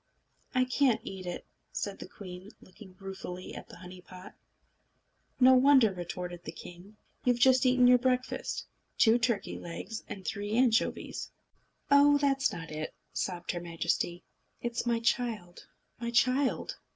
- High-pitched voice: Yes, high, 220 Hz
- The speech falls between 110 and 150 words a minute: Yes, average, 145 wpm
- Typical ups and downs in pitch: No, wide, 5.7 semitones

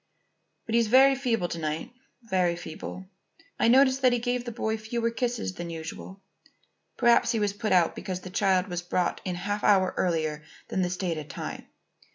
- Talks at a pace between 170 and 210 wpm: Yes, average, 190 wpm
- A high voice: Yes, high, 195 Hz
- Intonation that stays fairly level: No, average, 4.9 semitones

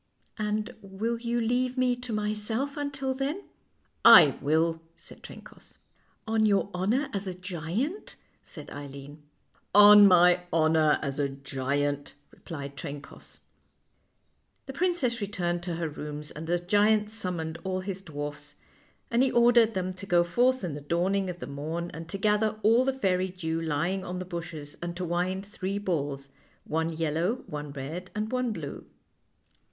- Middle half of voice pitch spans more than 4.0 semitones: Yes, average, 5.3 semitones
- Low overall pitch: No, medium, 185 Hz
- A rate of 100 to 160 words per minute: No, average, 170 wpm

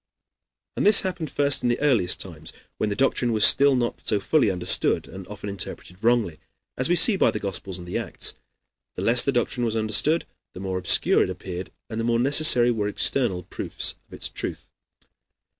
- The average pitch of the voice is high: No, low, 115 Hz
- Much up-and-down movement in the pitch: Yes, wide, 5.8 semitones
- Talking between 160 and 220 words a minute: Yes, average, 195 wpm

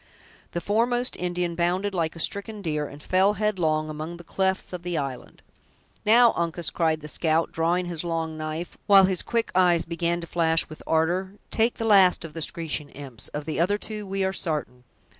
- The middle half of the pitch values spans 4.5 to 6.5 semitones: No, average, 3.2 semitones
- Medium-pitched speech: Yes, medium, 170 Hz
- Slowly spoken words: No, average, 195 wpm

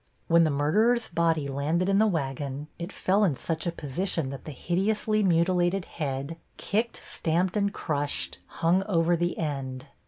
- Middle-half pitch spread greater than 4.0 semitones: Yes, average, 4.6 semitones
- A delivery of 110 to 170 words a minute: Yes, average, 160 wpm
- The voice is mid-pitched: Yes, medium, 170 Hz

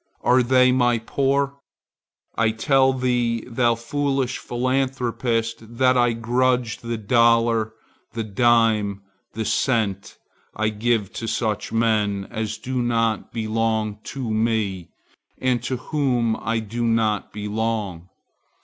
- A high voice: No, low, 115 Hz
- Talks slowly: Yes, slow, 120 wpm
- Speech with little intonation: Yes, narrow, 2.3 semitones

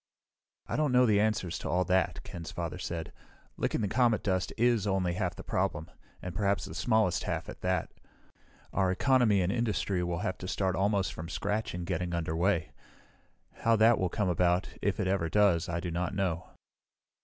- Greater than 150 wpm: Yes, average, 190 wpm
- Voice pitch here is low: Yes, very low, 95 Hz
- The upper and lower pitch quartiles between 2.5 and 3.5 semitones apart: Yes, average, 3.1 semitones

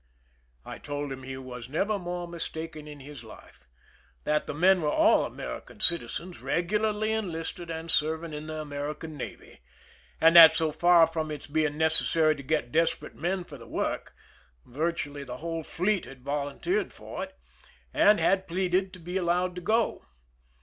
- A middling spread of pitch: Yes, average, 3.2 semitones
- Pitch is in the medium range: Yes, medium, 160 Hz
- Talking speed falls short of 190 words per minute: Yes, average, 170 wpm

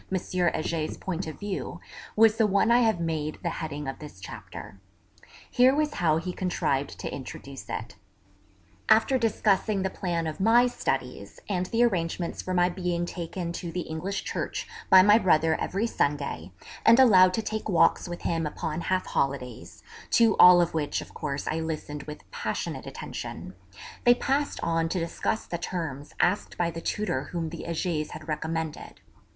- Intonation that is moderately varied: Yes, average, 4.3 semitones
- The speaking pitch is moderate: Yes, medium, 175 Hz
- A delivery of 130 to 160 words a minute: No, average, 170 wpm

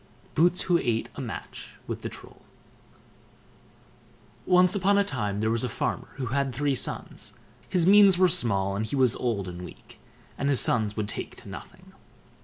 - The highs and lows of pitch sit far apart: Yes, wide, 8.5 semitones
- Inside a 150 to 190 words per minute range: Yes, average, 180 wpm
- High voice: No, low, 130 Hz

